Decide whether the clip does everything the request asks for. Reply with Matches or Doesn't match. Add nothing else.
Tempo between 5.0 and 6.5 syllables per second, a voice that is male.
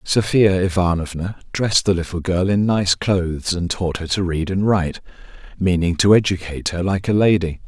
Matches